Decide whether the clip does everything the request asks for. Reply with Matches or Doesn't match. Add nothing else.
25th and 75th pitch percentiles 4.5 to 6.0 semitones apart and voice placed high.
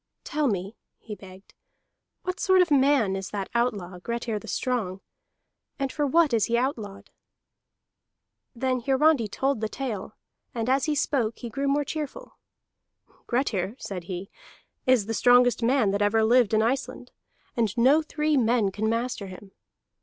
Matches